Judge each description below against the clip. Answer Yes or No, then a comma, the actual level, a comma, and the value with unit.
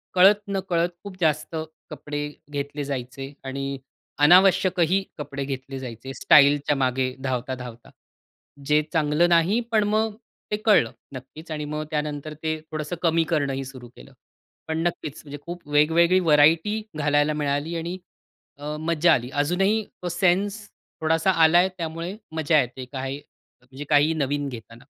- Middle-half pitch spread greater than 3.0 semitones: Yes, average, 3.7 semitones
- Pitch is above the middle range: No, medium, 150 Hz